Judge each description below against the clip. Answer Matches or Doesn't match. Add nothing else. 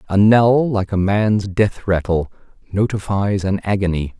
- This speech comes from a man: Matches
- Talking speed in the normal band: Matches